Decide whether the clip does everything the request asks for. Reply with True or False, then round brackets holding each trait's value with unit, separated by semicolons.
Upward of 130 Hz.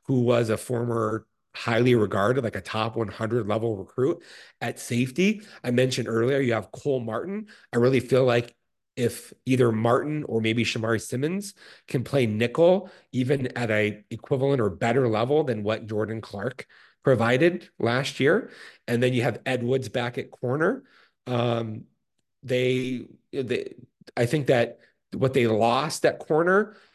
False (120 Hz)